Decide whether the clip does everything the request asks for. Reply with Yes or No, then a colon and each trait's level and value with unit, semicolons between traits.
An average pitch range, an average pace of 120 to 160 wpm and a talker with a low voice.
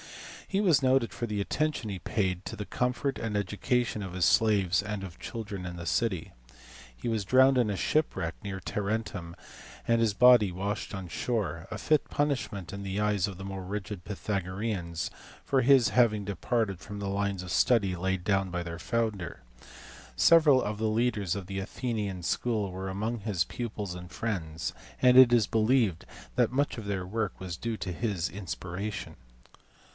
No: average, 3.7 semitones; average, 180 wpm; low, 105 Hz